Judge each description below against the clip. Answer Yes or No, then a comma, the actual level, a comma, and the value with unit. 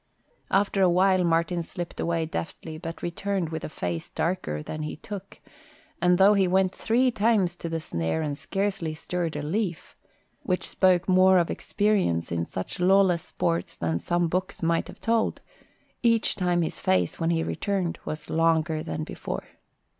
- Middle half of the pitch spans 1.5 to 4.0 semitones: Yes, average, 3.3 semitones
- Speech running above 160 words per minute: Yes, average, 170 wpm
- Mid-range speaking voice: Yes, medium, 175 Hz